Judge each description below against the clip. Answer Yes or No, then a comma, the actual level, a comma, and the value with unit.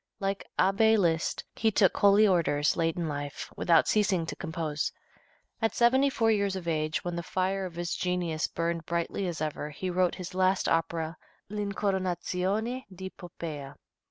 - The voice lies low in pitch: No, medium, 180 Hz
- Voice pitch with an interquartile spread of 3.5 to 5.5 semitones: No, average, 3.1 semitones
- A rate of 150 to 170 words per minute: Yes, average, 160 wpm